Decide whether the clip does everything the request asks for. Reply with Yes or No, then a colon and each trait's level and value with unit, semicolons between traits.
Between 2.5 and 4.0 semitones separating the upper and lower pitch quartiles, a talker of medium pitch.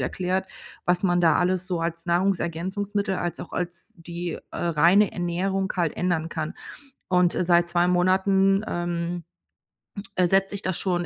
No: narrow, 1.8 semitones; medium, 180 Hz